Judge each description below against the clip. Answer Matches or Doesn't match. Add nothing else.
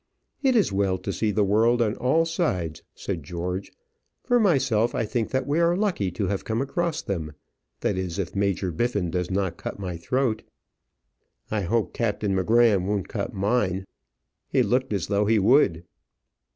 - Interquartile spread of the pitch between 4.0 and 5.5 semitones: Matches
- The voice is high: Doesn't match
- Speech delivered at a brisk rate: Doesn't match